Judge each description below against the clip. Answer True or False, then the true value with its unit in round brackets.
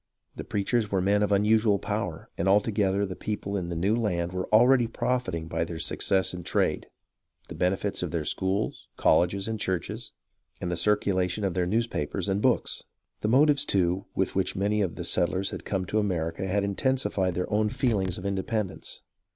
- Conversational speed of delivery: True (190 wpm)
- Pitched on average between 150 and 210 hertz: False (100 Hz)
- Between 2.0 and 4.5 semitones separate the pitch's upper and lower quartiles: True (2.8 semitones)